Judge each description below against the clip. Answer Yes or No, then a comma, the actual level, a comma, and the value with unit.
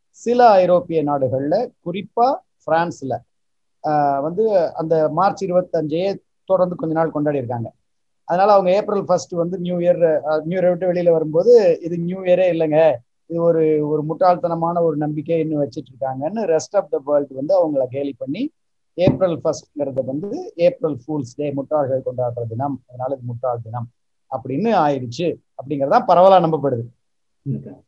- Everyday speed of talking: No, fast, 140 wpm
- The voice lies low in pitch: No, medium, 160 Hz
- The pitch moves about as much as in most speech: Yes, average, 4.4 semitones